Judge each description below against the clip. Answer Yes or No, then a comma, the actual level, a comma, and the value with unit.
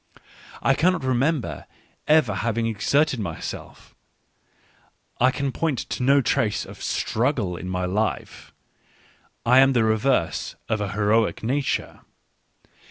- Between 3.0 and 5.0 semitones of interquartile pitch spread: Yes, average, 4.6 semitones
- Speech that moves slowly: Yes, slow, 120 wpm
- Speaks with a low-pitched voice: Yes, low, 120 Hz